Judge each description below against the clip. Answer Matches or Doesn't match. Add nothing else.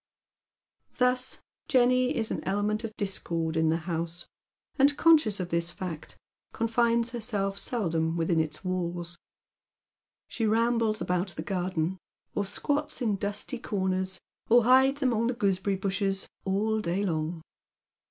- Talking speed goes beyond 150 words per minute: Doesn't match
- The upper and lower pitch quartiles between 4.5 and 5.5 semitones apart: Matches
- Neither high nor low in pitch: Doesn't match